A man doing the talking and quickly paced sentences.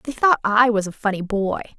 No: female; fast, 235 wpm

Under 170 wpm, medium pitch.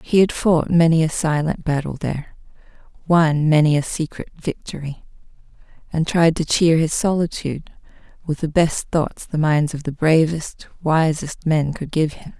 Yes: average, 160 wpm; medium, 155 Hz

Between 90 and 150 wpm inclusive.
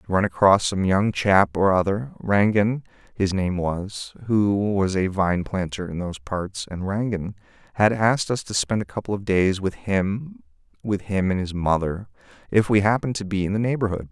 No: average, 185 wpm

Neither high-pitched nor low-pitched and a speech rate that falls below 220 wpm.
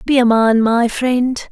No: high, 240 Hz; average, 200 wpm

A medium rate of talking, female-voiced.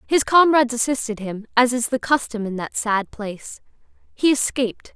Yes: average, 170 wpm; female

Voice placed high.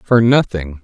No: low, 105 Hz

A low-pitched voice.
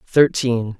Yes: low, 120 Hz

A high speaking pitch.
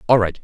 No: low, 105 Hz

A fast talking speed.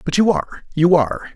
Yes: fast, 220 wpm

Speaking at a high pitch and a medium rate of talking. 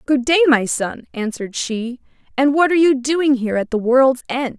No: very high, 260 Hz; fast, 210 wpm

